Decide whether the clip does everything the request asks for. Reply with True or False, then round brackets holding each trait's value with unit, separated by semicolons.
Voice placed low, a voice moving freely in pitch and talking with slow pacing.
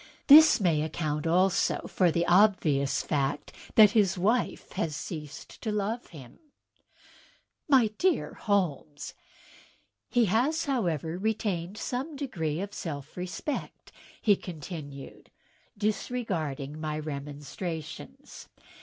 False (180 Hz; 6.2 semitones; 100 wpm)